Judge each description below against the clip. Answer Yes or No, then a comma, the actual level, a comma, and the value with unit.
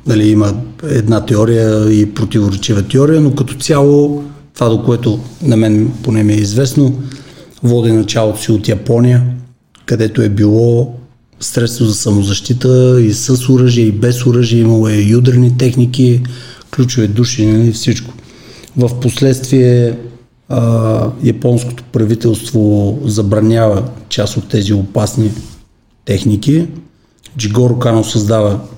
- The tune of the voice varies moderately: No, narrow, 2.3 semitones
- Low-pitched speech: Yes, low, 115 Hz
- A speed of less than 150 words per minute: Yes, average, 120 wpm